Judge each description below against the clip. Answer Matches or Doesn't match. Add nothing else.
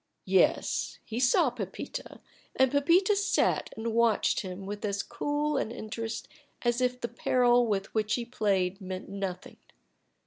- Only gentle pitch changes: Doesn't match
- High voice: Matches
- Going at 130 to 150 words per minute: Matches